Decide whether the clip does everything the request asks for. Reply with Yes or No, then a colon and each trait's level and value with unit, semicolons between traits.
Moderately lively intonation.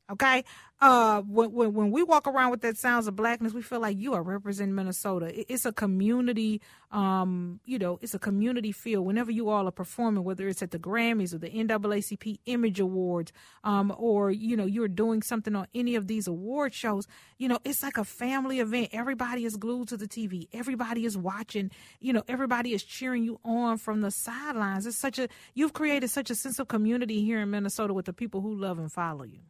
Yes: average, 3.3 semitones